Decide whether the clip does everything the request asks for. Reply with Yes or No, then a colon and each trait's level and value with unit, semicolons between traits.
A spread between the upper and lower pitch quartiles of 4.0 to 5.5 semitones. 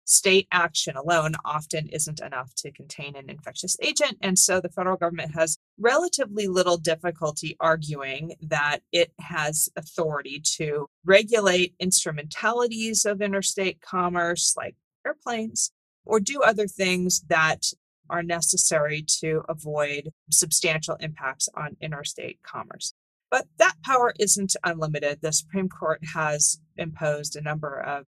No: average, 3.5 semitones